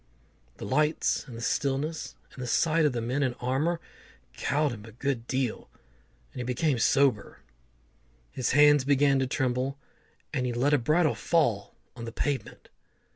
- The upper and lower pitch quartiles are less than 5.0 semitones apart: Yes, average, 3.2 semitones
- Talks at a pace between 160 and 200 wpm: Yes, average, 165 wpm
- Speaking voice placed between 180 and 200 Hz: No, low, 135 Hz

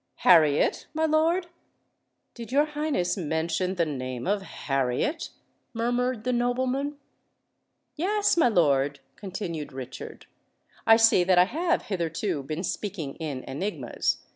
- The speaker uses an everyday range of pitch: No, wide, 8.9 semitones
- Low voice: No, high, 195 Hz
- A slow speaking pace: Yes, slow, 115 wpm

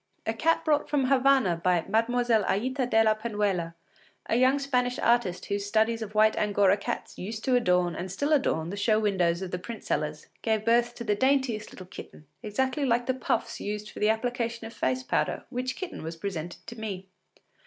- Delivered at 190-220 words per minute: Yes, average, 195 wpm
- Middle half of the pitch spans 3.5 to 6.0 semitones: Yes, average, 4.0 semitones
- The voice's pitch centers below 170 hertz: No, high, 220 Hz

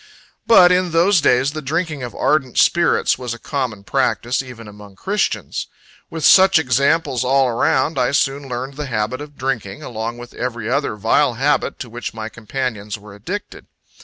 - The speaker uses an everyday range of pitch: Yes, average, 4.2 semitones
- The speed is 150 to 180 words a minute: Yes, average, 170 wpm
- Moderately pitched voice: No, low, 130 Hz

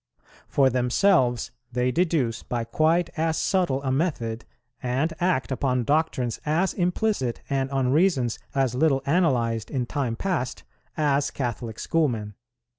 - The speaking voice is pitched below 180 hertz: Yes, low, 135 Hz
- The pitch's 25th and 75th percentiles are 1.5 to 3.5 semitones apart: No, average, 4.7 semitones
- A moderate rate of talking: No, slow, 130 wpm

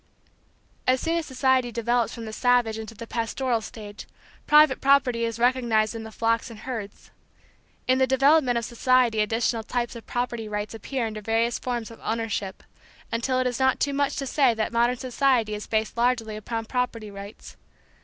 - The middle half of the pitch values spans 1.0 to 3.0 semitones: Yes, narrow, 2.5 semitones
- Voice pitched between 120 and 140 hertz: No, high, 235 Hz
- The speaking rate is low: No, average, 180 wpm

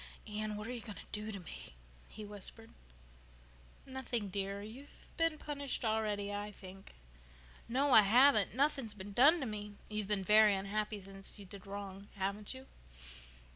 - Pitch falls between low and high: No, high, 210 Hz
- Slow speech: No, average, 170 wpm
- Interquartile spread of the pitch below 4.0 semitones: Yes, average, 3.0 semitones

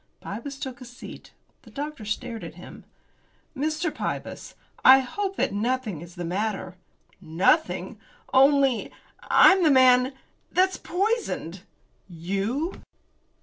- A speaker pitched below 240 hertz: No, very high, 255 Hz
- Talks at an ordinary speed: No, slow, 115 wpm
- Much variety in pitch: Yes, wide, 6.9 semitones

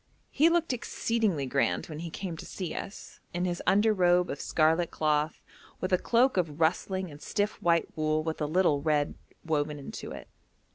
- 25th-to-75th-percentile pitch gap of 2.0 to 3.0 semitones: No, average, 3.7 semitones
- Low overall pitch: No, medium, 170 Hz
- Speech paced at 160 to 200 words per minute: Yes, average, 185 wpm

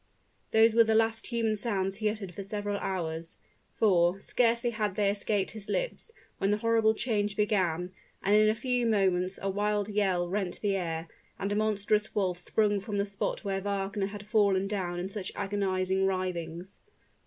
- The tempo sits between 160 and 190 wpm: Yes, average, 175 wpm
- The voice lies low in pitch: No, high, 200 Hz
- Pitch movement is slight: Yes, narrow, 2.1 semitones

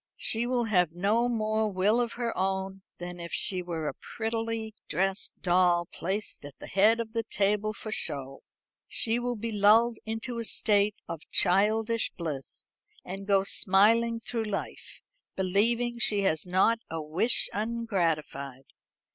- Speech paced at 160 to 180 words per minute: No, average, 150 wpm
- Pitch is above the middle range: Yes, high, 205 Hz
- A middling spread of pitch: Yes, average, 4.1 semitones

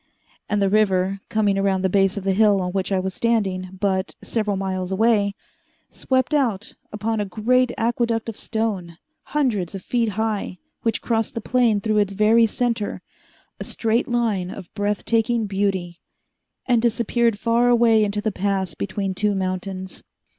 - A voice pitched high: Yes, high, 210 Hz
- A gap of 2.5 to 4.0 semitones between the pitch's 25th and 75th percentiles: Yes, average, 3.0 semitones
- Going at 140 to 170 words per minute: Yes, average, 165 wpm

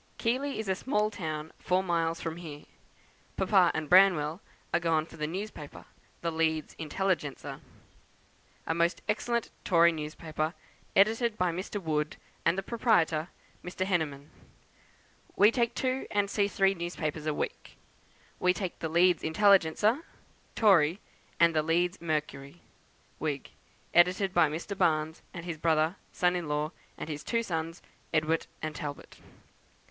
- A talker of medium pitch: Yes, medium, 170 Hz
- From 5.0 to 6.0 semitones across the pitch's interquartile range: No, average, 3.7 semitones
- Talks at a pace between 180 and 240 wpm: No, average, 140 wpm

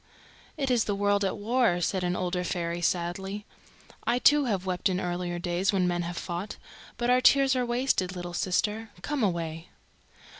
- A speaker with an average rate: Yes, average, 180 wpm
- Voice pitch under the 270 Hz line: Yes, high, 190 Hz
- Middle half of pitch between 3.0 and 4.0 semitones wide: No, average, 4.7 semitones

